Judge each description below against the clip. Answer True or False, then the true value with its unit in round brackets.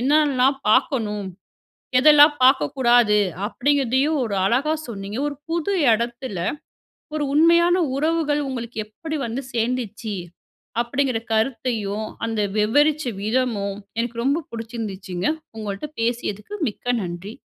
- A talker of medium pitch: False (245 Hz)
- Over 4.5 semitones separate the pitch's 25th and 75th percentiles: True (5.0 semitones)